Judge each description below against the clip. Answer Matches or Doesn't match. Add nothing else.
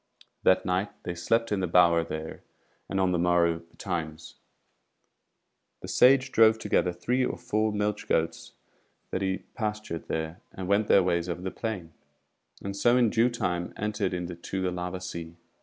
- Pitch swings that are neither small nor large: Matches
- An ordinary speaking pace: Matches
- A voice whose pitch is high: Doesn't match